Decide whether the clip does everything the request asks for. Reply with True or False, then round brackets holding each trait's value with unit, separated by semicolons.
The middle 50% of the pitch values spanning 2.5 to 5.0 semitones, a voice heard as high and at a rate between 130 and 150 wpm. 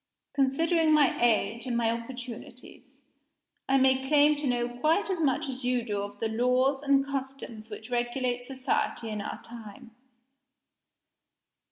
True (2.8 semitones; 250 Hz; 145 wpm)